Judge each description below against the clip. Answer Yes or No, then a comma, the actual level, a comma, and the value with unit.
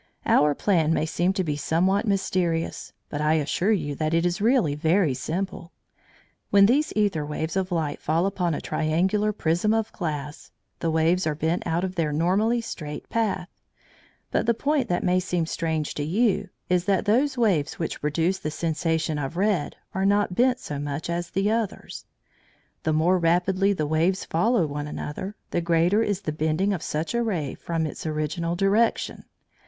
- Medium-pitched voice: Yes, medium, 175 Hz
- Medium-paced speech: Yes, average, 180 wpm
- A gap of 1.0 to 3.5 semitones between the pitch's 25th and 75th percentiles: No, average, 4.1 semitones